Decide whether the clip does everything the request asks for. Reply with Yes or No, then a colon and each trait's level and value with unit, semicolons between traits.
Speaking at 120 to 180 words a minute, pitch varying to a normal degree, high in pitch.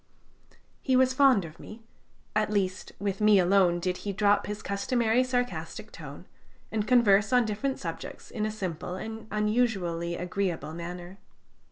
Yes: average, 150 wpm; average, 3.5 semitones; high, 205 Hz